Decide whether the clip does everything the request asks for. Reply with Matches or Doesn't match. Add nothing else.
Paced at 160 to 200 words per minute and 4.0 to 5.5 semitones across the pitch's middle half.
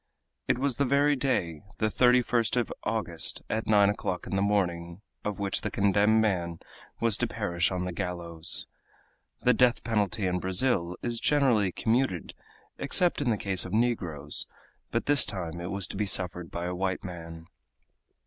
Matches